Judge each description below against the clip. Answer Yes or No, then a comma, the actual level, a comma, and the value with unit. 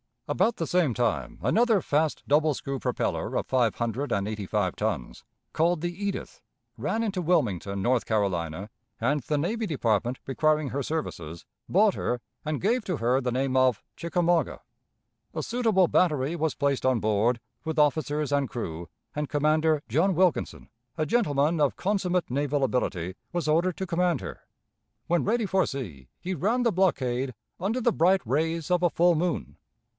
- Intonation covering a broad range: Yes, wide, 6.0 semitones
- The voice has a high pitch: No, medium, 150 Hz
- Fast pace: No, average, 165 wpm